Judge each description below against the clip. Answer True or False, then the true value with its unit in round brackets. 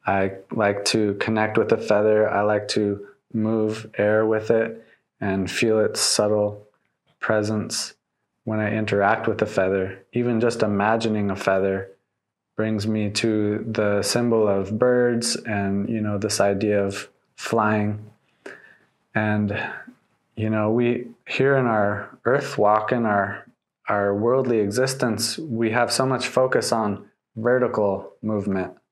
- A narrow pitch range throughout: True (1.8 semitones)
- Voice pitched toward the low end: True (110 Hz)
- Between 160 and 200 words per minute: False (135 wpm)